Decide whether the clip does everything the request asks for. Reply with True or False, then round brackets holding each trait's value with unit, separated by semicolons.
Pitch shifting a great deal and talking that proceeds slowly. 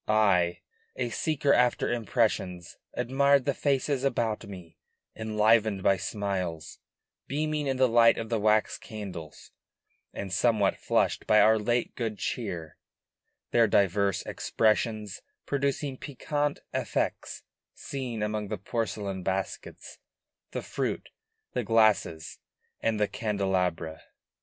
False (3.8 semitones; 115 wpm)